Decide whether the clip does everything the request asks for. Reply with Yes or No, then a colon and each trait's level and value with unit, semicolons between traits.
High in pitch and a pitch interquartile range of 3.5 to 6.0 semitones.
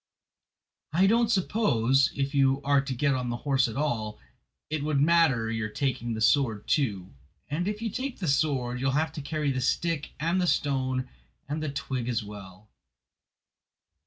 No: medium, 140 Hz; average, 4.3 semitones